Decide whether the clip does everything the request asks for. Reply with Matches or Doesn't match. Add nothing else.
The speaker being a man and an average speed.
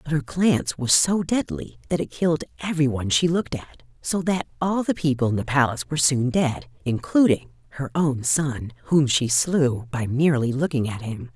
Doesn't match